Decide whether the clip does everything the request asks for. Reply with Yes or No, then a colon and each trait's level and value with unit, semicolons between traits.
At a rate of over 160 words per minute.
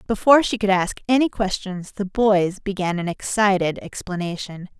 No: average, 150 wpm